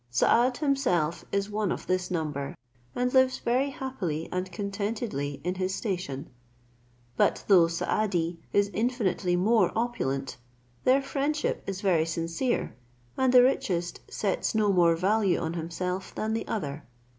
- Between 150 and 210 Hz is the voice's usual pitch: Yes, high, 190 Hz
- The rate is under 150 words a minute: Yes, average, 140 wpm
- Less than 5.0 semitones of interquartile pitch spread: No, wide, 5.6 semitones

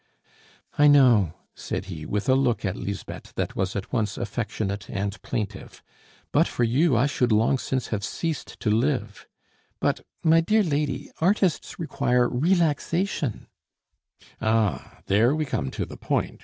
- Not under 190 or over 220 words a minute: No, average, 155 wpm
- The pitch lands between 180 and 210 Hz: No, low, 120 Hz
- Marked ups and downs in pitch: Yes, wide, 6.0 semitones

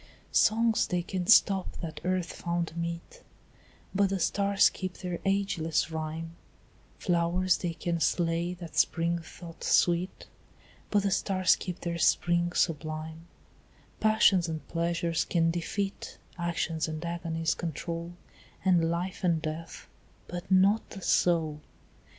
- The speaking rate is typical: No, slow, 125 wpm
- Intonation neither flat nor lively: No, narrow, 2.0 semitones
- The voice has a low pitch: No, medium, 170 Hz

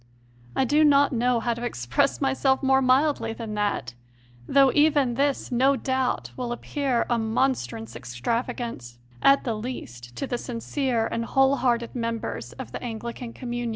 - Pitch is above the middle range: Yes, high, 240 Hz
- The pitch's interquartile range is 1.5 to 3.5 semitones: Yes, average, 3.1 semitones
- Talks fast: No, average, 160 wpm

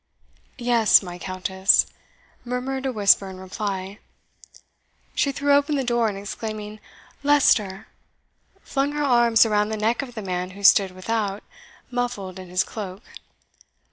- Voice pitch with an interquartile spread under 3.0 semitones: No, average, 4.2 semitones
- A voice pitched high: Yes, high, 215 Hz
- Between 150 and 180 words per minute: No, average, 140 wpm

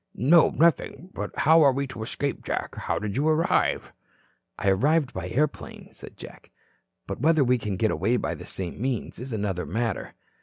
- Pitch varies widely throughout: Yes, wide, 6.4 semitones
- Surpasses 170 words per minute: Yes, average, 185 wpm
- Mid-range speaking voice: No, low, 125 Hz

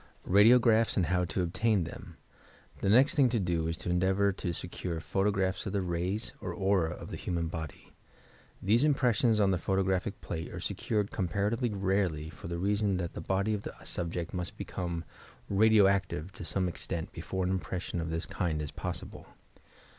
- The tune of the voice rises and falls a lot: No, average, 3.0 semitones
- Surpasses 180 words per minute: Yes, average, 190 wpm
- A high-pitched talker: No, very low, 95 Hz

